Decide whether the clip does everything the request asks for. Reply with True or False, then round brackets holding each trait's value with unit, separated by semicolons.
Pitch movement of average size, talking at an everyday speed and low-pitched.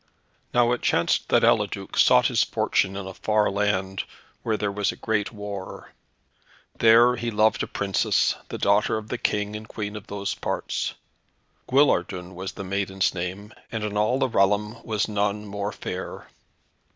False (1.8 semitones; 165 wpm; 105 Hz)